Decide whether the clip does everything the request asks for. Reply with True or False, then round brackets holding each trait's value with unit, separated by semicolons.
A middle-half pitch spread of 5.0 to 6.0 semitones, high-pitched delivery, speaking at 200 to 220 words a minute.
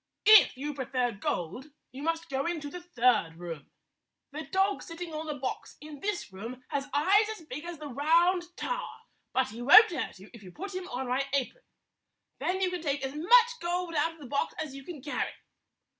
True (5.3 semitones; 295 Hz; 205 wpm)